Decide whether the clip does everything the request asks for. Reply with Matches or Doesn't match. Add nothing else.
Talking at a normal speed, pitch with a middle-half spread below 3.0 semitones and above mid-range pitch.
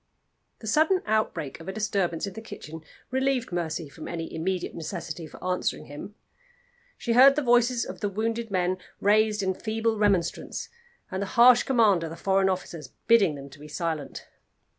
Doesn't match